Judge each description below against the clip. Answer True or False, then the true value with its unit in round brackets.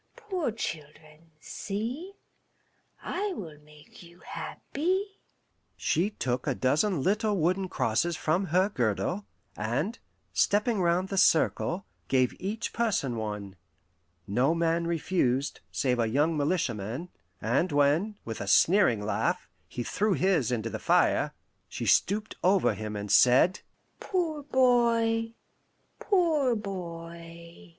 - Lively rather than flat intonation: True (7.8 semitones)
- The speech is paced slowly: True (120 wpm)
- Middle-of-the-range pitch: True (170 Hz)